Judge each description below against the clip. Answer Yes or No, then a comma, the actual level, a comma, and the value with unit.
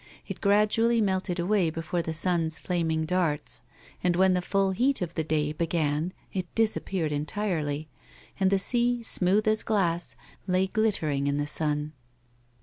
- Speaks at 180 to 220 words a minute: No, average, 150 wpm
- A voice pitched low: No, medium, 180 Hz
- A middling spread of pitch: Yes, average, 4.0 semitones